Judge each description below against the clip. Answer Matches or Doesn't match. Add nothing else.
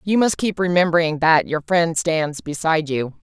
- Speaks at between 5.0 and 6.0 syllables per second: Doesn't match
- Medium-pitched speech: Matches